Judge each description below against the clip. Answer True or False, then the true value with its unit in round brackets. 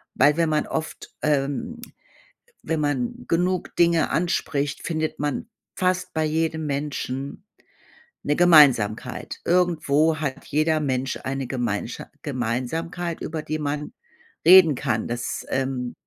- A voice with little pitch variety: False (3.5 semitones)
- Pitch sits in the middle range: True (150 Hz)